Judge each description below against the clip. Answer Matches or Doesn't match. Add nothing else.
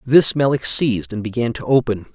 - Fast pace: Doesn't match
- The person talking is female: Doesn't match